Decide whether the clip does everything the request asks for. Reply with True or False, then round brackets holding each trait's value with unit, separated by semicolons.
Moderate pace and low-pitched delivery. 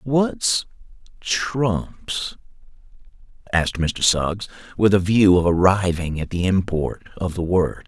False (120 wpm; 95 Hz)